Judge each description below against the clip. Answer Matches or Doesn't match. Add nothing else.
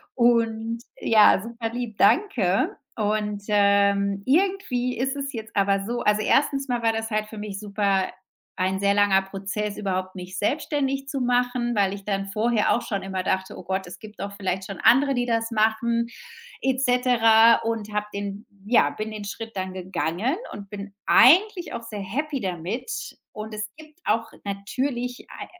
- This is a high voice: Matches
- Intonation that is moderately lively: Matches